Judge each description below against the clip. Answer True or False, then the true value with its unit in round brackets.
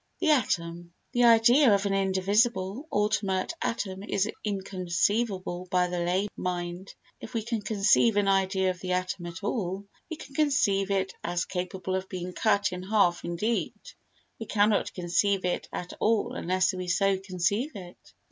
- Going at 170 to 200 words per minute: False (160 wpm)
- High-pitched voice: True (195 Hz)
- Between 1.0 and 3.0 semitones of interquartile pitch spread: True (2.6 semitones)